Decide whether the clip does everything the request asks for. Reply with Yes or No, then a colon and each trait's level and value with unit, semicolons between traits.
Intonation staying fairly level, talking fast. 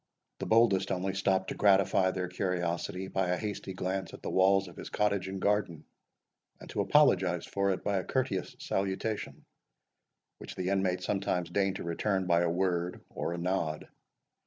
No: narrow, 1.6 semitones; average, 175 wpm